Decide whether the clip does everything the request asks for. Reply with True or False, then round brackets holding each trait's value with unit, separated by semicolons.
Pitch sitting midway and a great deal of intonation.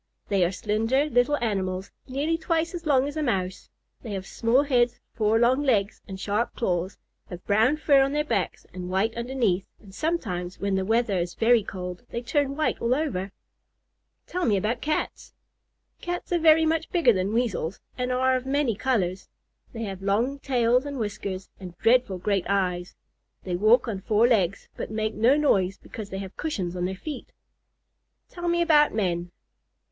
False (225 Hz; 6.1 semitones)